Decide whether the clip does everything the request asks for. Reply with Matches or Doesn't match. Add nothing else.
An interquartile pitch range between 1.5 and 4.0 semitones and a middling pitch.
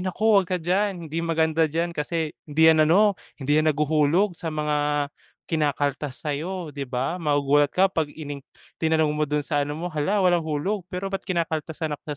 Matches